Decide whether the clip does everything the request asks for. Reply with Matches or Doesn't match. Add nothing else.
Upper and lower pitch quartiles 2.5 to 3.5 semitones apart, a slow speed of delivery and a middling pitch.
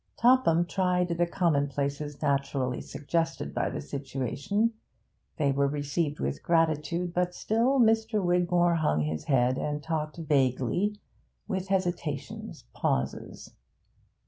Doesn't match